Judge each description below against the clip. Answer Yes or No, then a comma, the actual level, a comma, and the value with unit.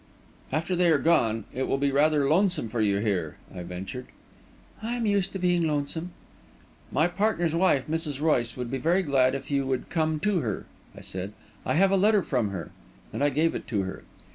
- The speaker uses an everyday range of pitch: No, wide, 6.1 semitones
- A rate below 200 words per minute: No, fast, 205 wpm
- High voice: No, medium, 145 Hz